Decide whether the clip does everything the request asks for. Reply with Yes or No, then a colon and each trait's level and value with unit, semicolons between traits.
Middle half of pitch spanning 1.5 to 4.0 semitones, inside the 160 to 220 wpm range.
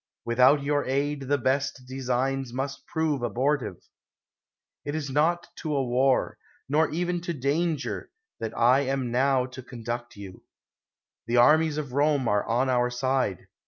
No: average, 2.9 semitones; average, 150 wpm